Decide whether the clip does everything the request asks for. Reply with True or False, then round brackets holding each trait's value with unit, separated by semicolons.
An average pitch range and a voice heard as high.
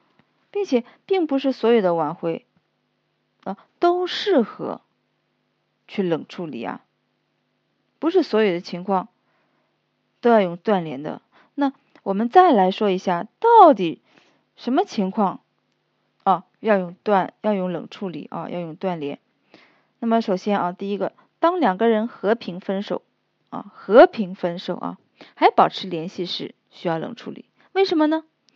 False (6.6 semitones; 210 Hz)